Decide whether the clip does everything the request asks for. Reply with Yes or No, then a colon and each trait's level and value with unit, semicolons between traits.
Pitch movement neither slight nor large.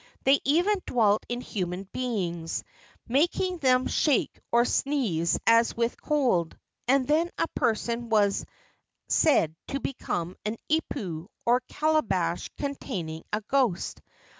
No: wide, 6.7 semitones